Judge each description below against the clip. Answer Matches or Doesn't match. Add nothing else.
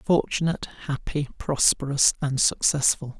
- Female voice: Doesn't match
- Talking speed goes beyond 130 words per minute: Doesn't match